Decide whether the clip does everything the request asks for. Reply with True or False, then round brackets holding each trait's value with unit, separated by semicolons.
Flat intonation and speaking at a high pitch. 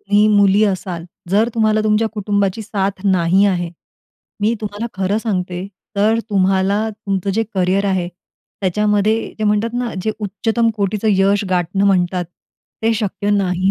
True (2.1 semitones; 200 Hz)